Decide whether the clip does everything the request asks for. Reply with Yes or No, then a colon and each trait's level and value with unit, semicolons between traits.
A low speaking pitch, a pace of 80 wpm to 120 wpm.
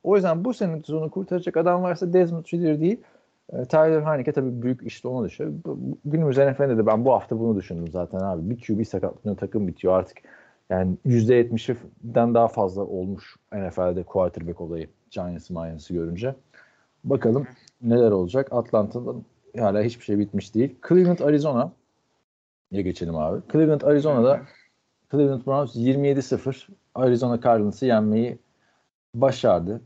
No: low, 120 Hz; average, 135 wpm